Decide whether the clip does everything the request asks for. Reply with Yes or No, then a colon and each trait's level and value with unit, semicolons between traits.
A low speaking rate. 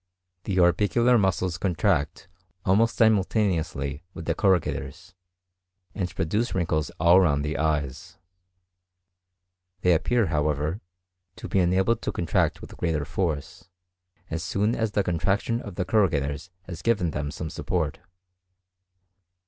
Yes: slow, 125 wpm